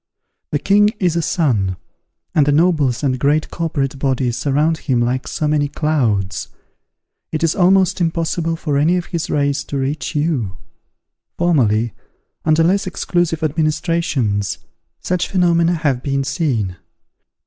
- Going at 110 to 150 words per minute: Yes, slow, 135 wpm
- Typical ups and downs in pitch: Yes, average, 3.9 semitones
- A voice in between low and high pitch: Yes, medium, 150 Hz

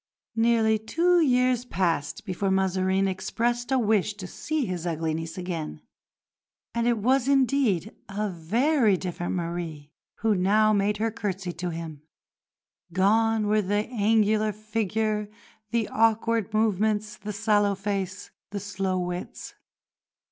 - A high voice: Yes, high, 210 Hz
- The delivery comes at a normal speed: No, slow, 130 wpm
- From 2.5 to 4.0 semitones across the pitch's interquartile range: Yes, average, 3.3 semitones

